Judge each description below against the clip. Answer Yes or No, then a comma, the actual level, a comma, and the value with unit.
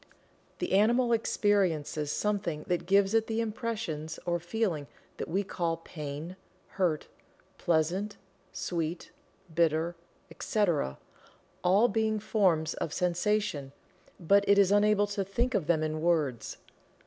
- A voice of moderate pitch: Yes, medium, 180 Hz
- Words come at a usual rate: No, slow, 125 wpm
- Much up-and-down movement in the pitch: No, average, 4.6 semitones